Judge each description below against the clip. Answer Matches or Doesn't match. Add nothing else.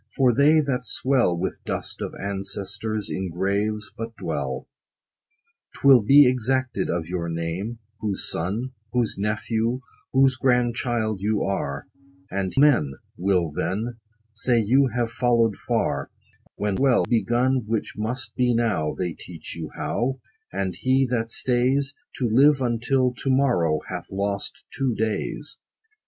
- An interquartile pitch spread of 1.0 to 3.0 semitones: Doesn't match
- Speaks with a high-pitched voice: Doesn't match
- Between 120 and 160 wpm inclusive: Matches